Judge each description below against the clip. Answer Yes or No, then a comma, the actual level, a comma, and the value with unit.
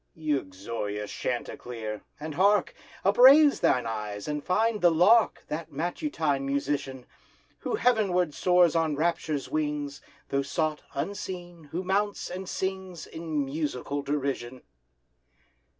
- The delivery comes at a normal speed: No, slow, 115 wpm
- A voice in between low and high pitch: Yes, medium, 155 Hz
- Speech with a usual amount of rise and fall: Yes, average, 4.8 semitones